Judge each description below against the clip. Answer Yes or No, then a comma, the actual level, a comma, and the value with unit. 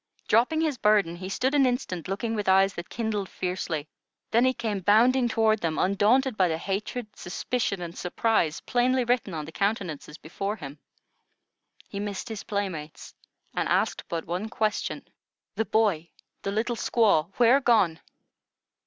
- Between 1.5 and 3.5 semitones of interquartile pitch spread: No, average, 4.7 semitones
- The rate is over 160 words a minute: No, average, 155 wpm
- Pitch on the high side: Yes, high, 205 Hz